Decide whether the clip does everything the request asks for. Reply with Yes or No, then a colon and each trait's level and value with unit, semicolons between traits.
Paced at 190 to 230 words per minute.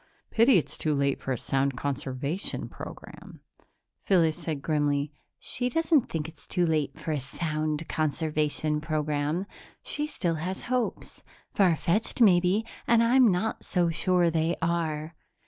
No: average, 145 wpm